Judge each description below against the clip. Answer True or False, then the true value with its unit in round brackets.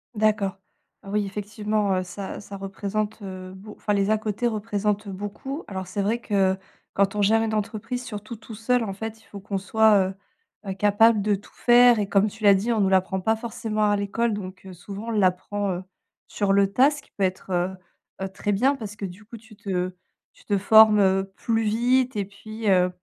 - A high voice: True (205 Hz)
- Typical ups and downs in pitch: False (2.1 semitones)